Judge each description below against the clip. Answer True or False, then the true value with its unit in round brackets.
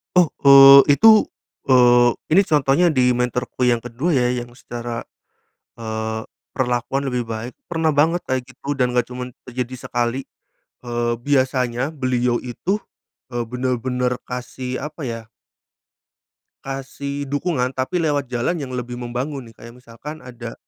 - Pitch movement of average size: False (2.3 semitones)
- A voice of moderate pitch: False (125 Hz)